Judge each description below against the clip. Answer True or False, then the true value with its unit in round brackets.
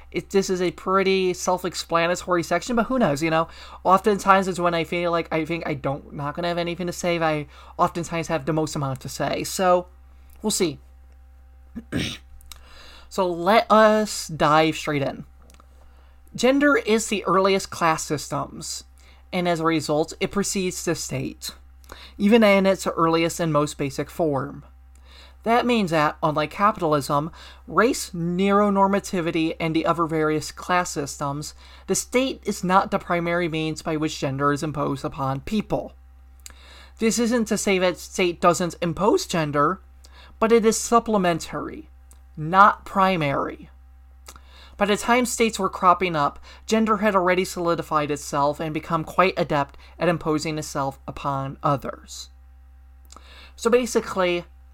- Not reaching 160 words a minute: True (145 wpm)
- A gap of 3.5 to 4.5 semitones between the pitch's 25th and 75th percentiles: False (5.5 semitones)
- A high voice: False (165 Hz)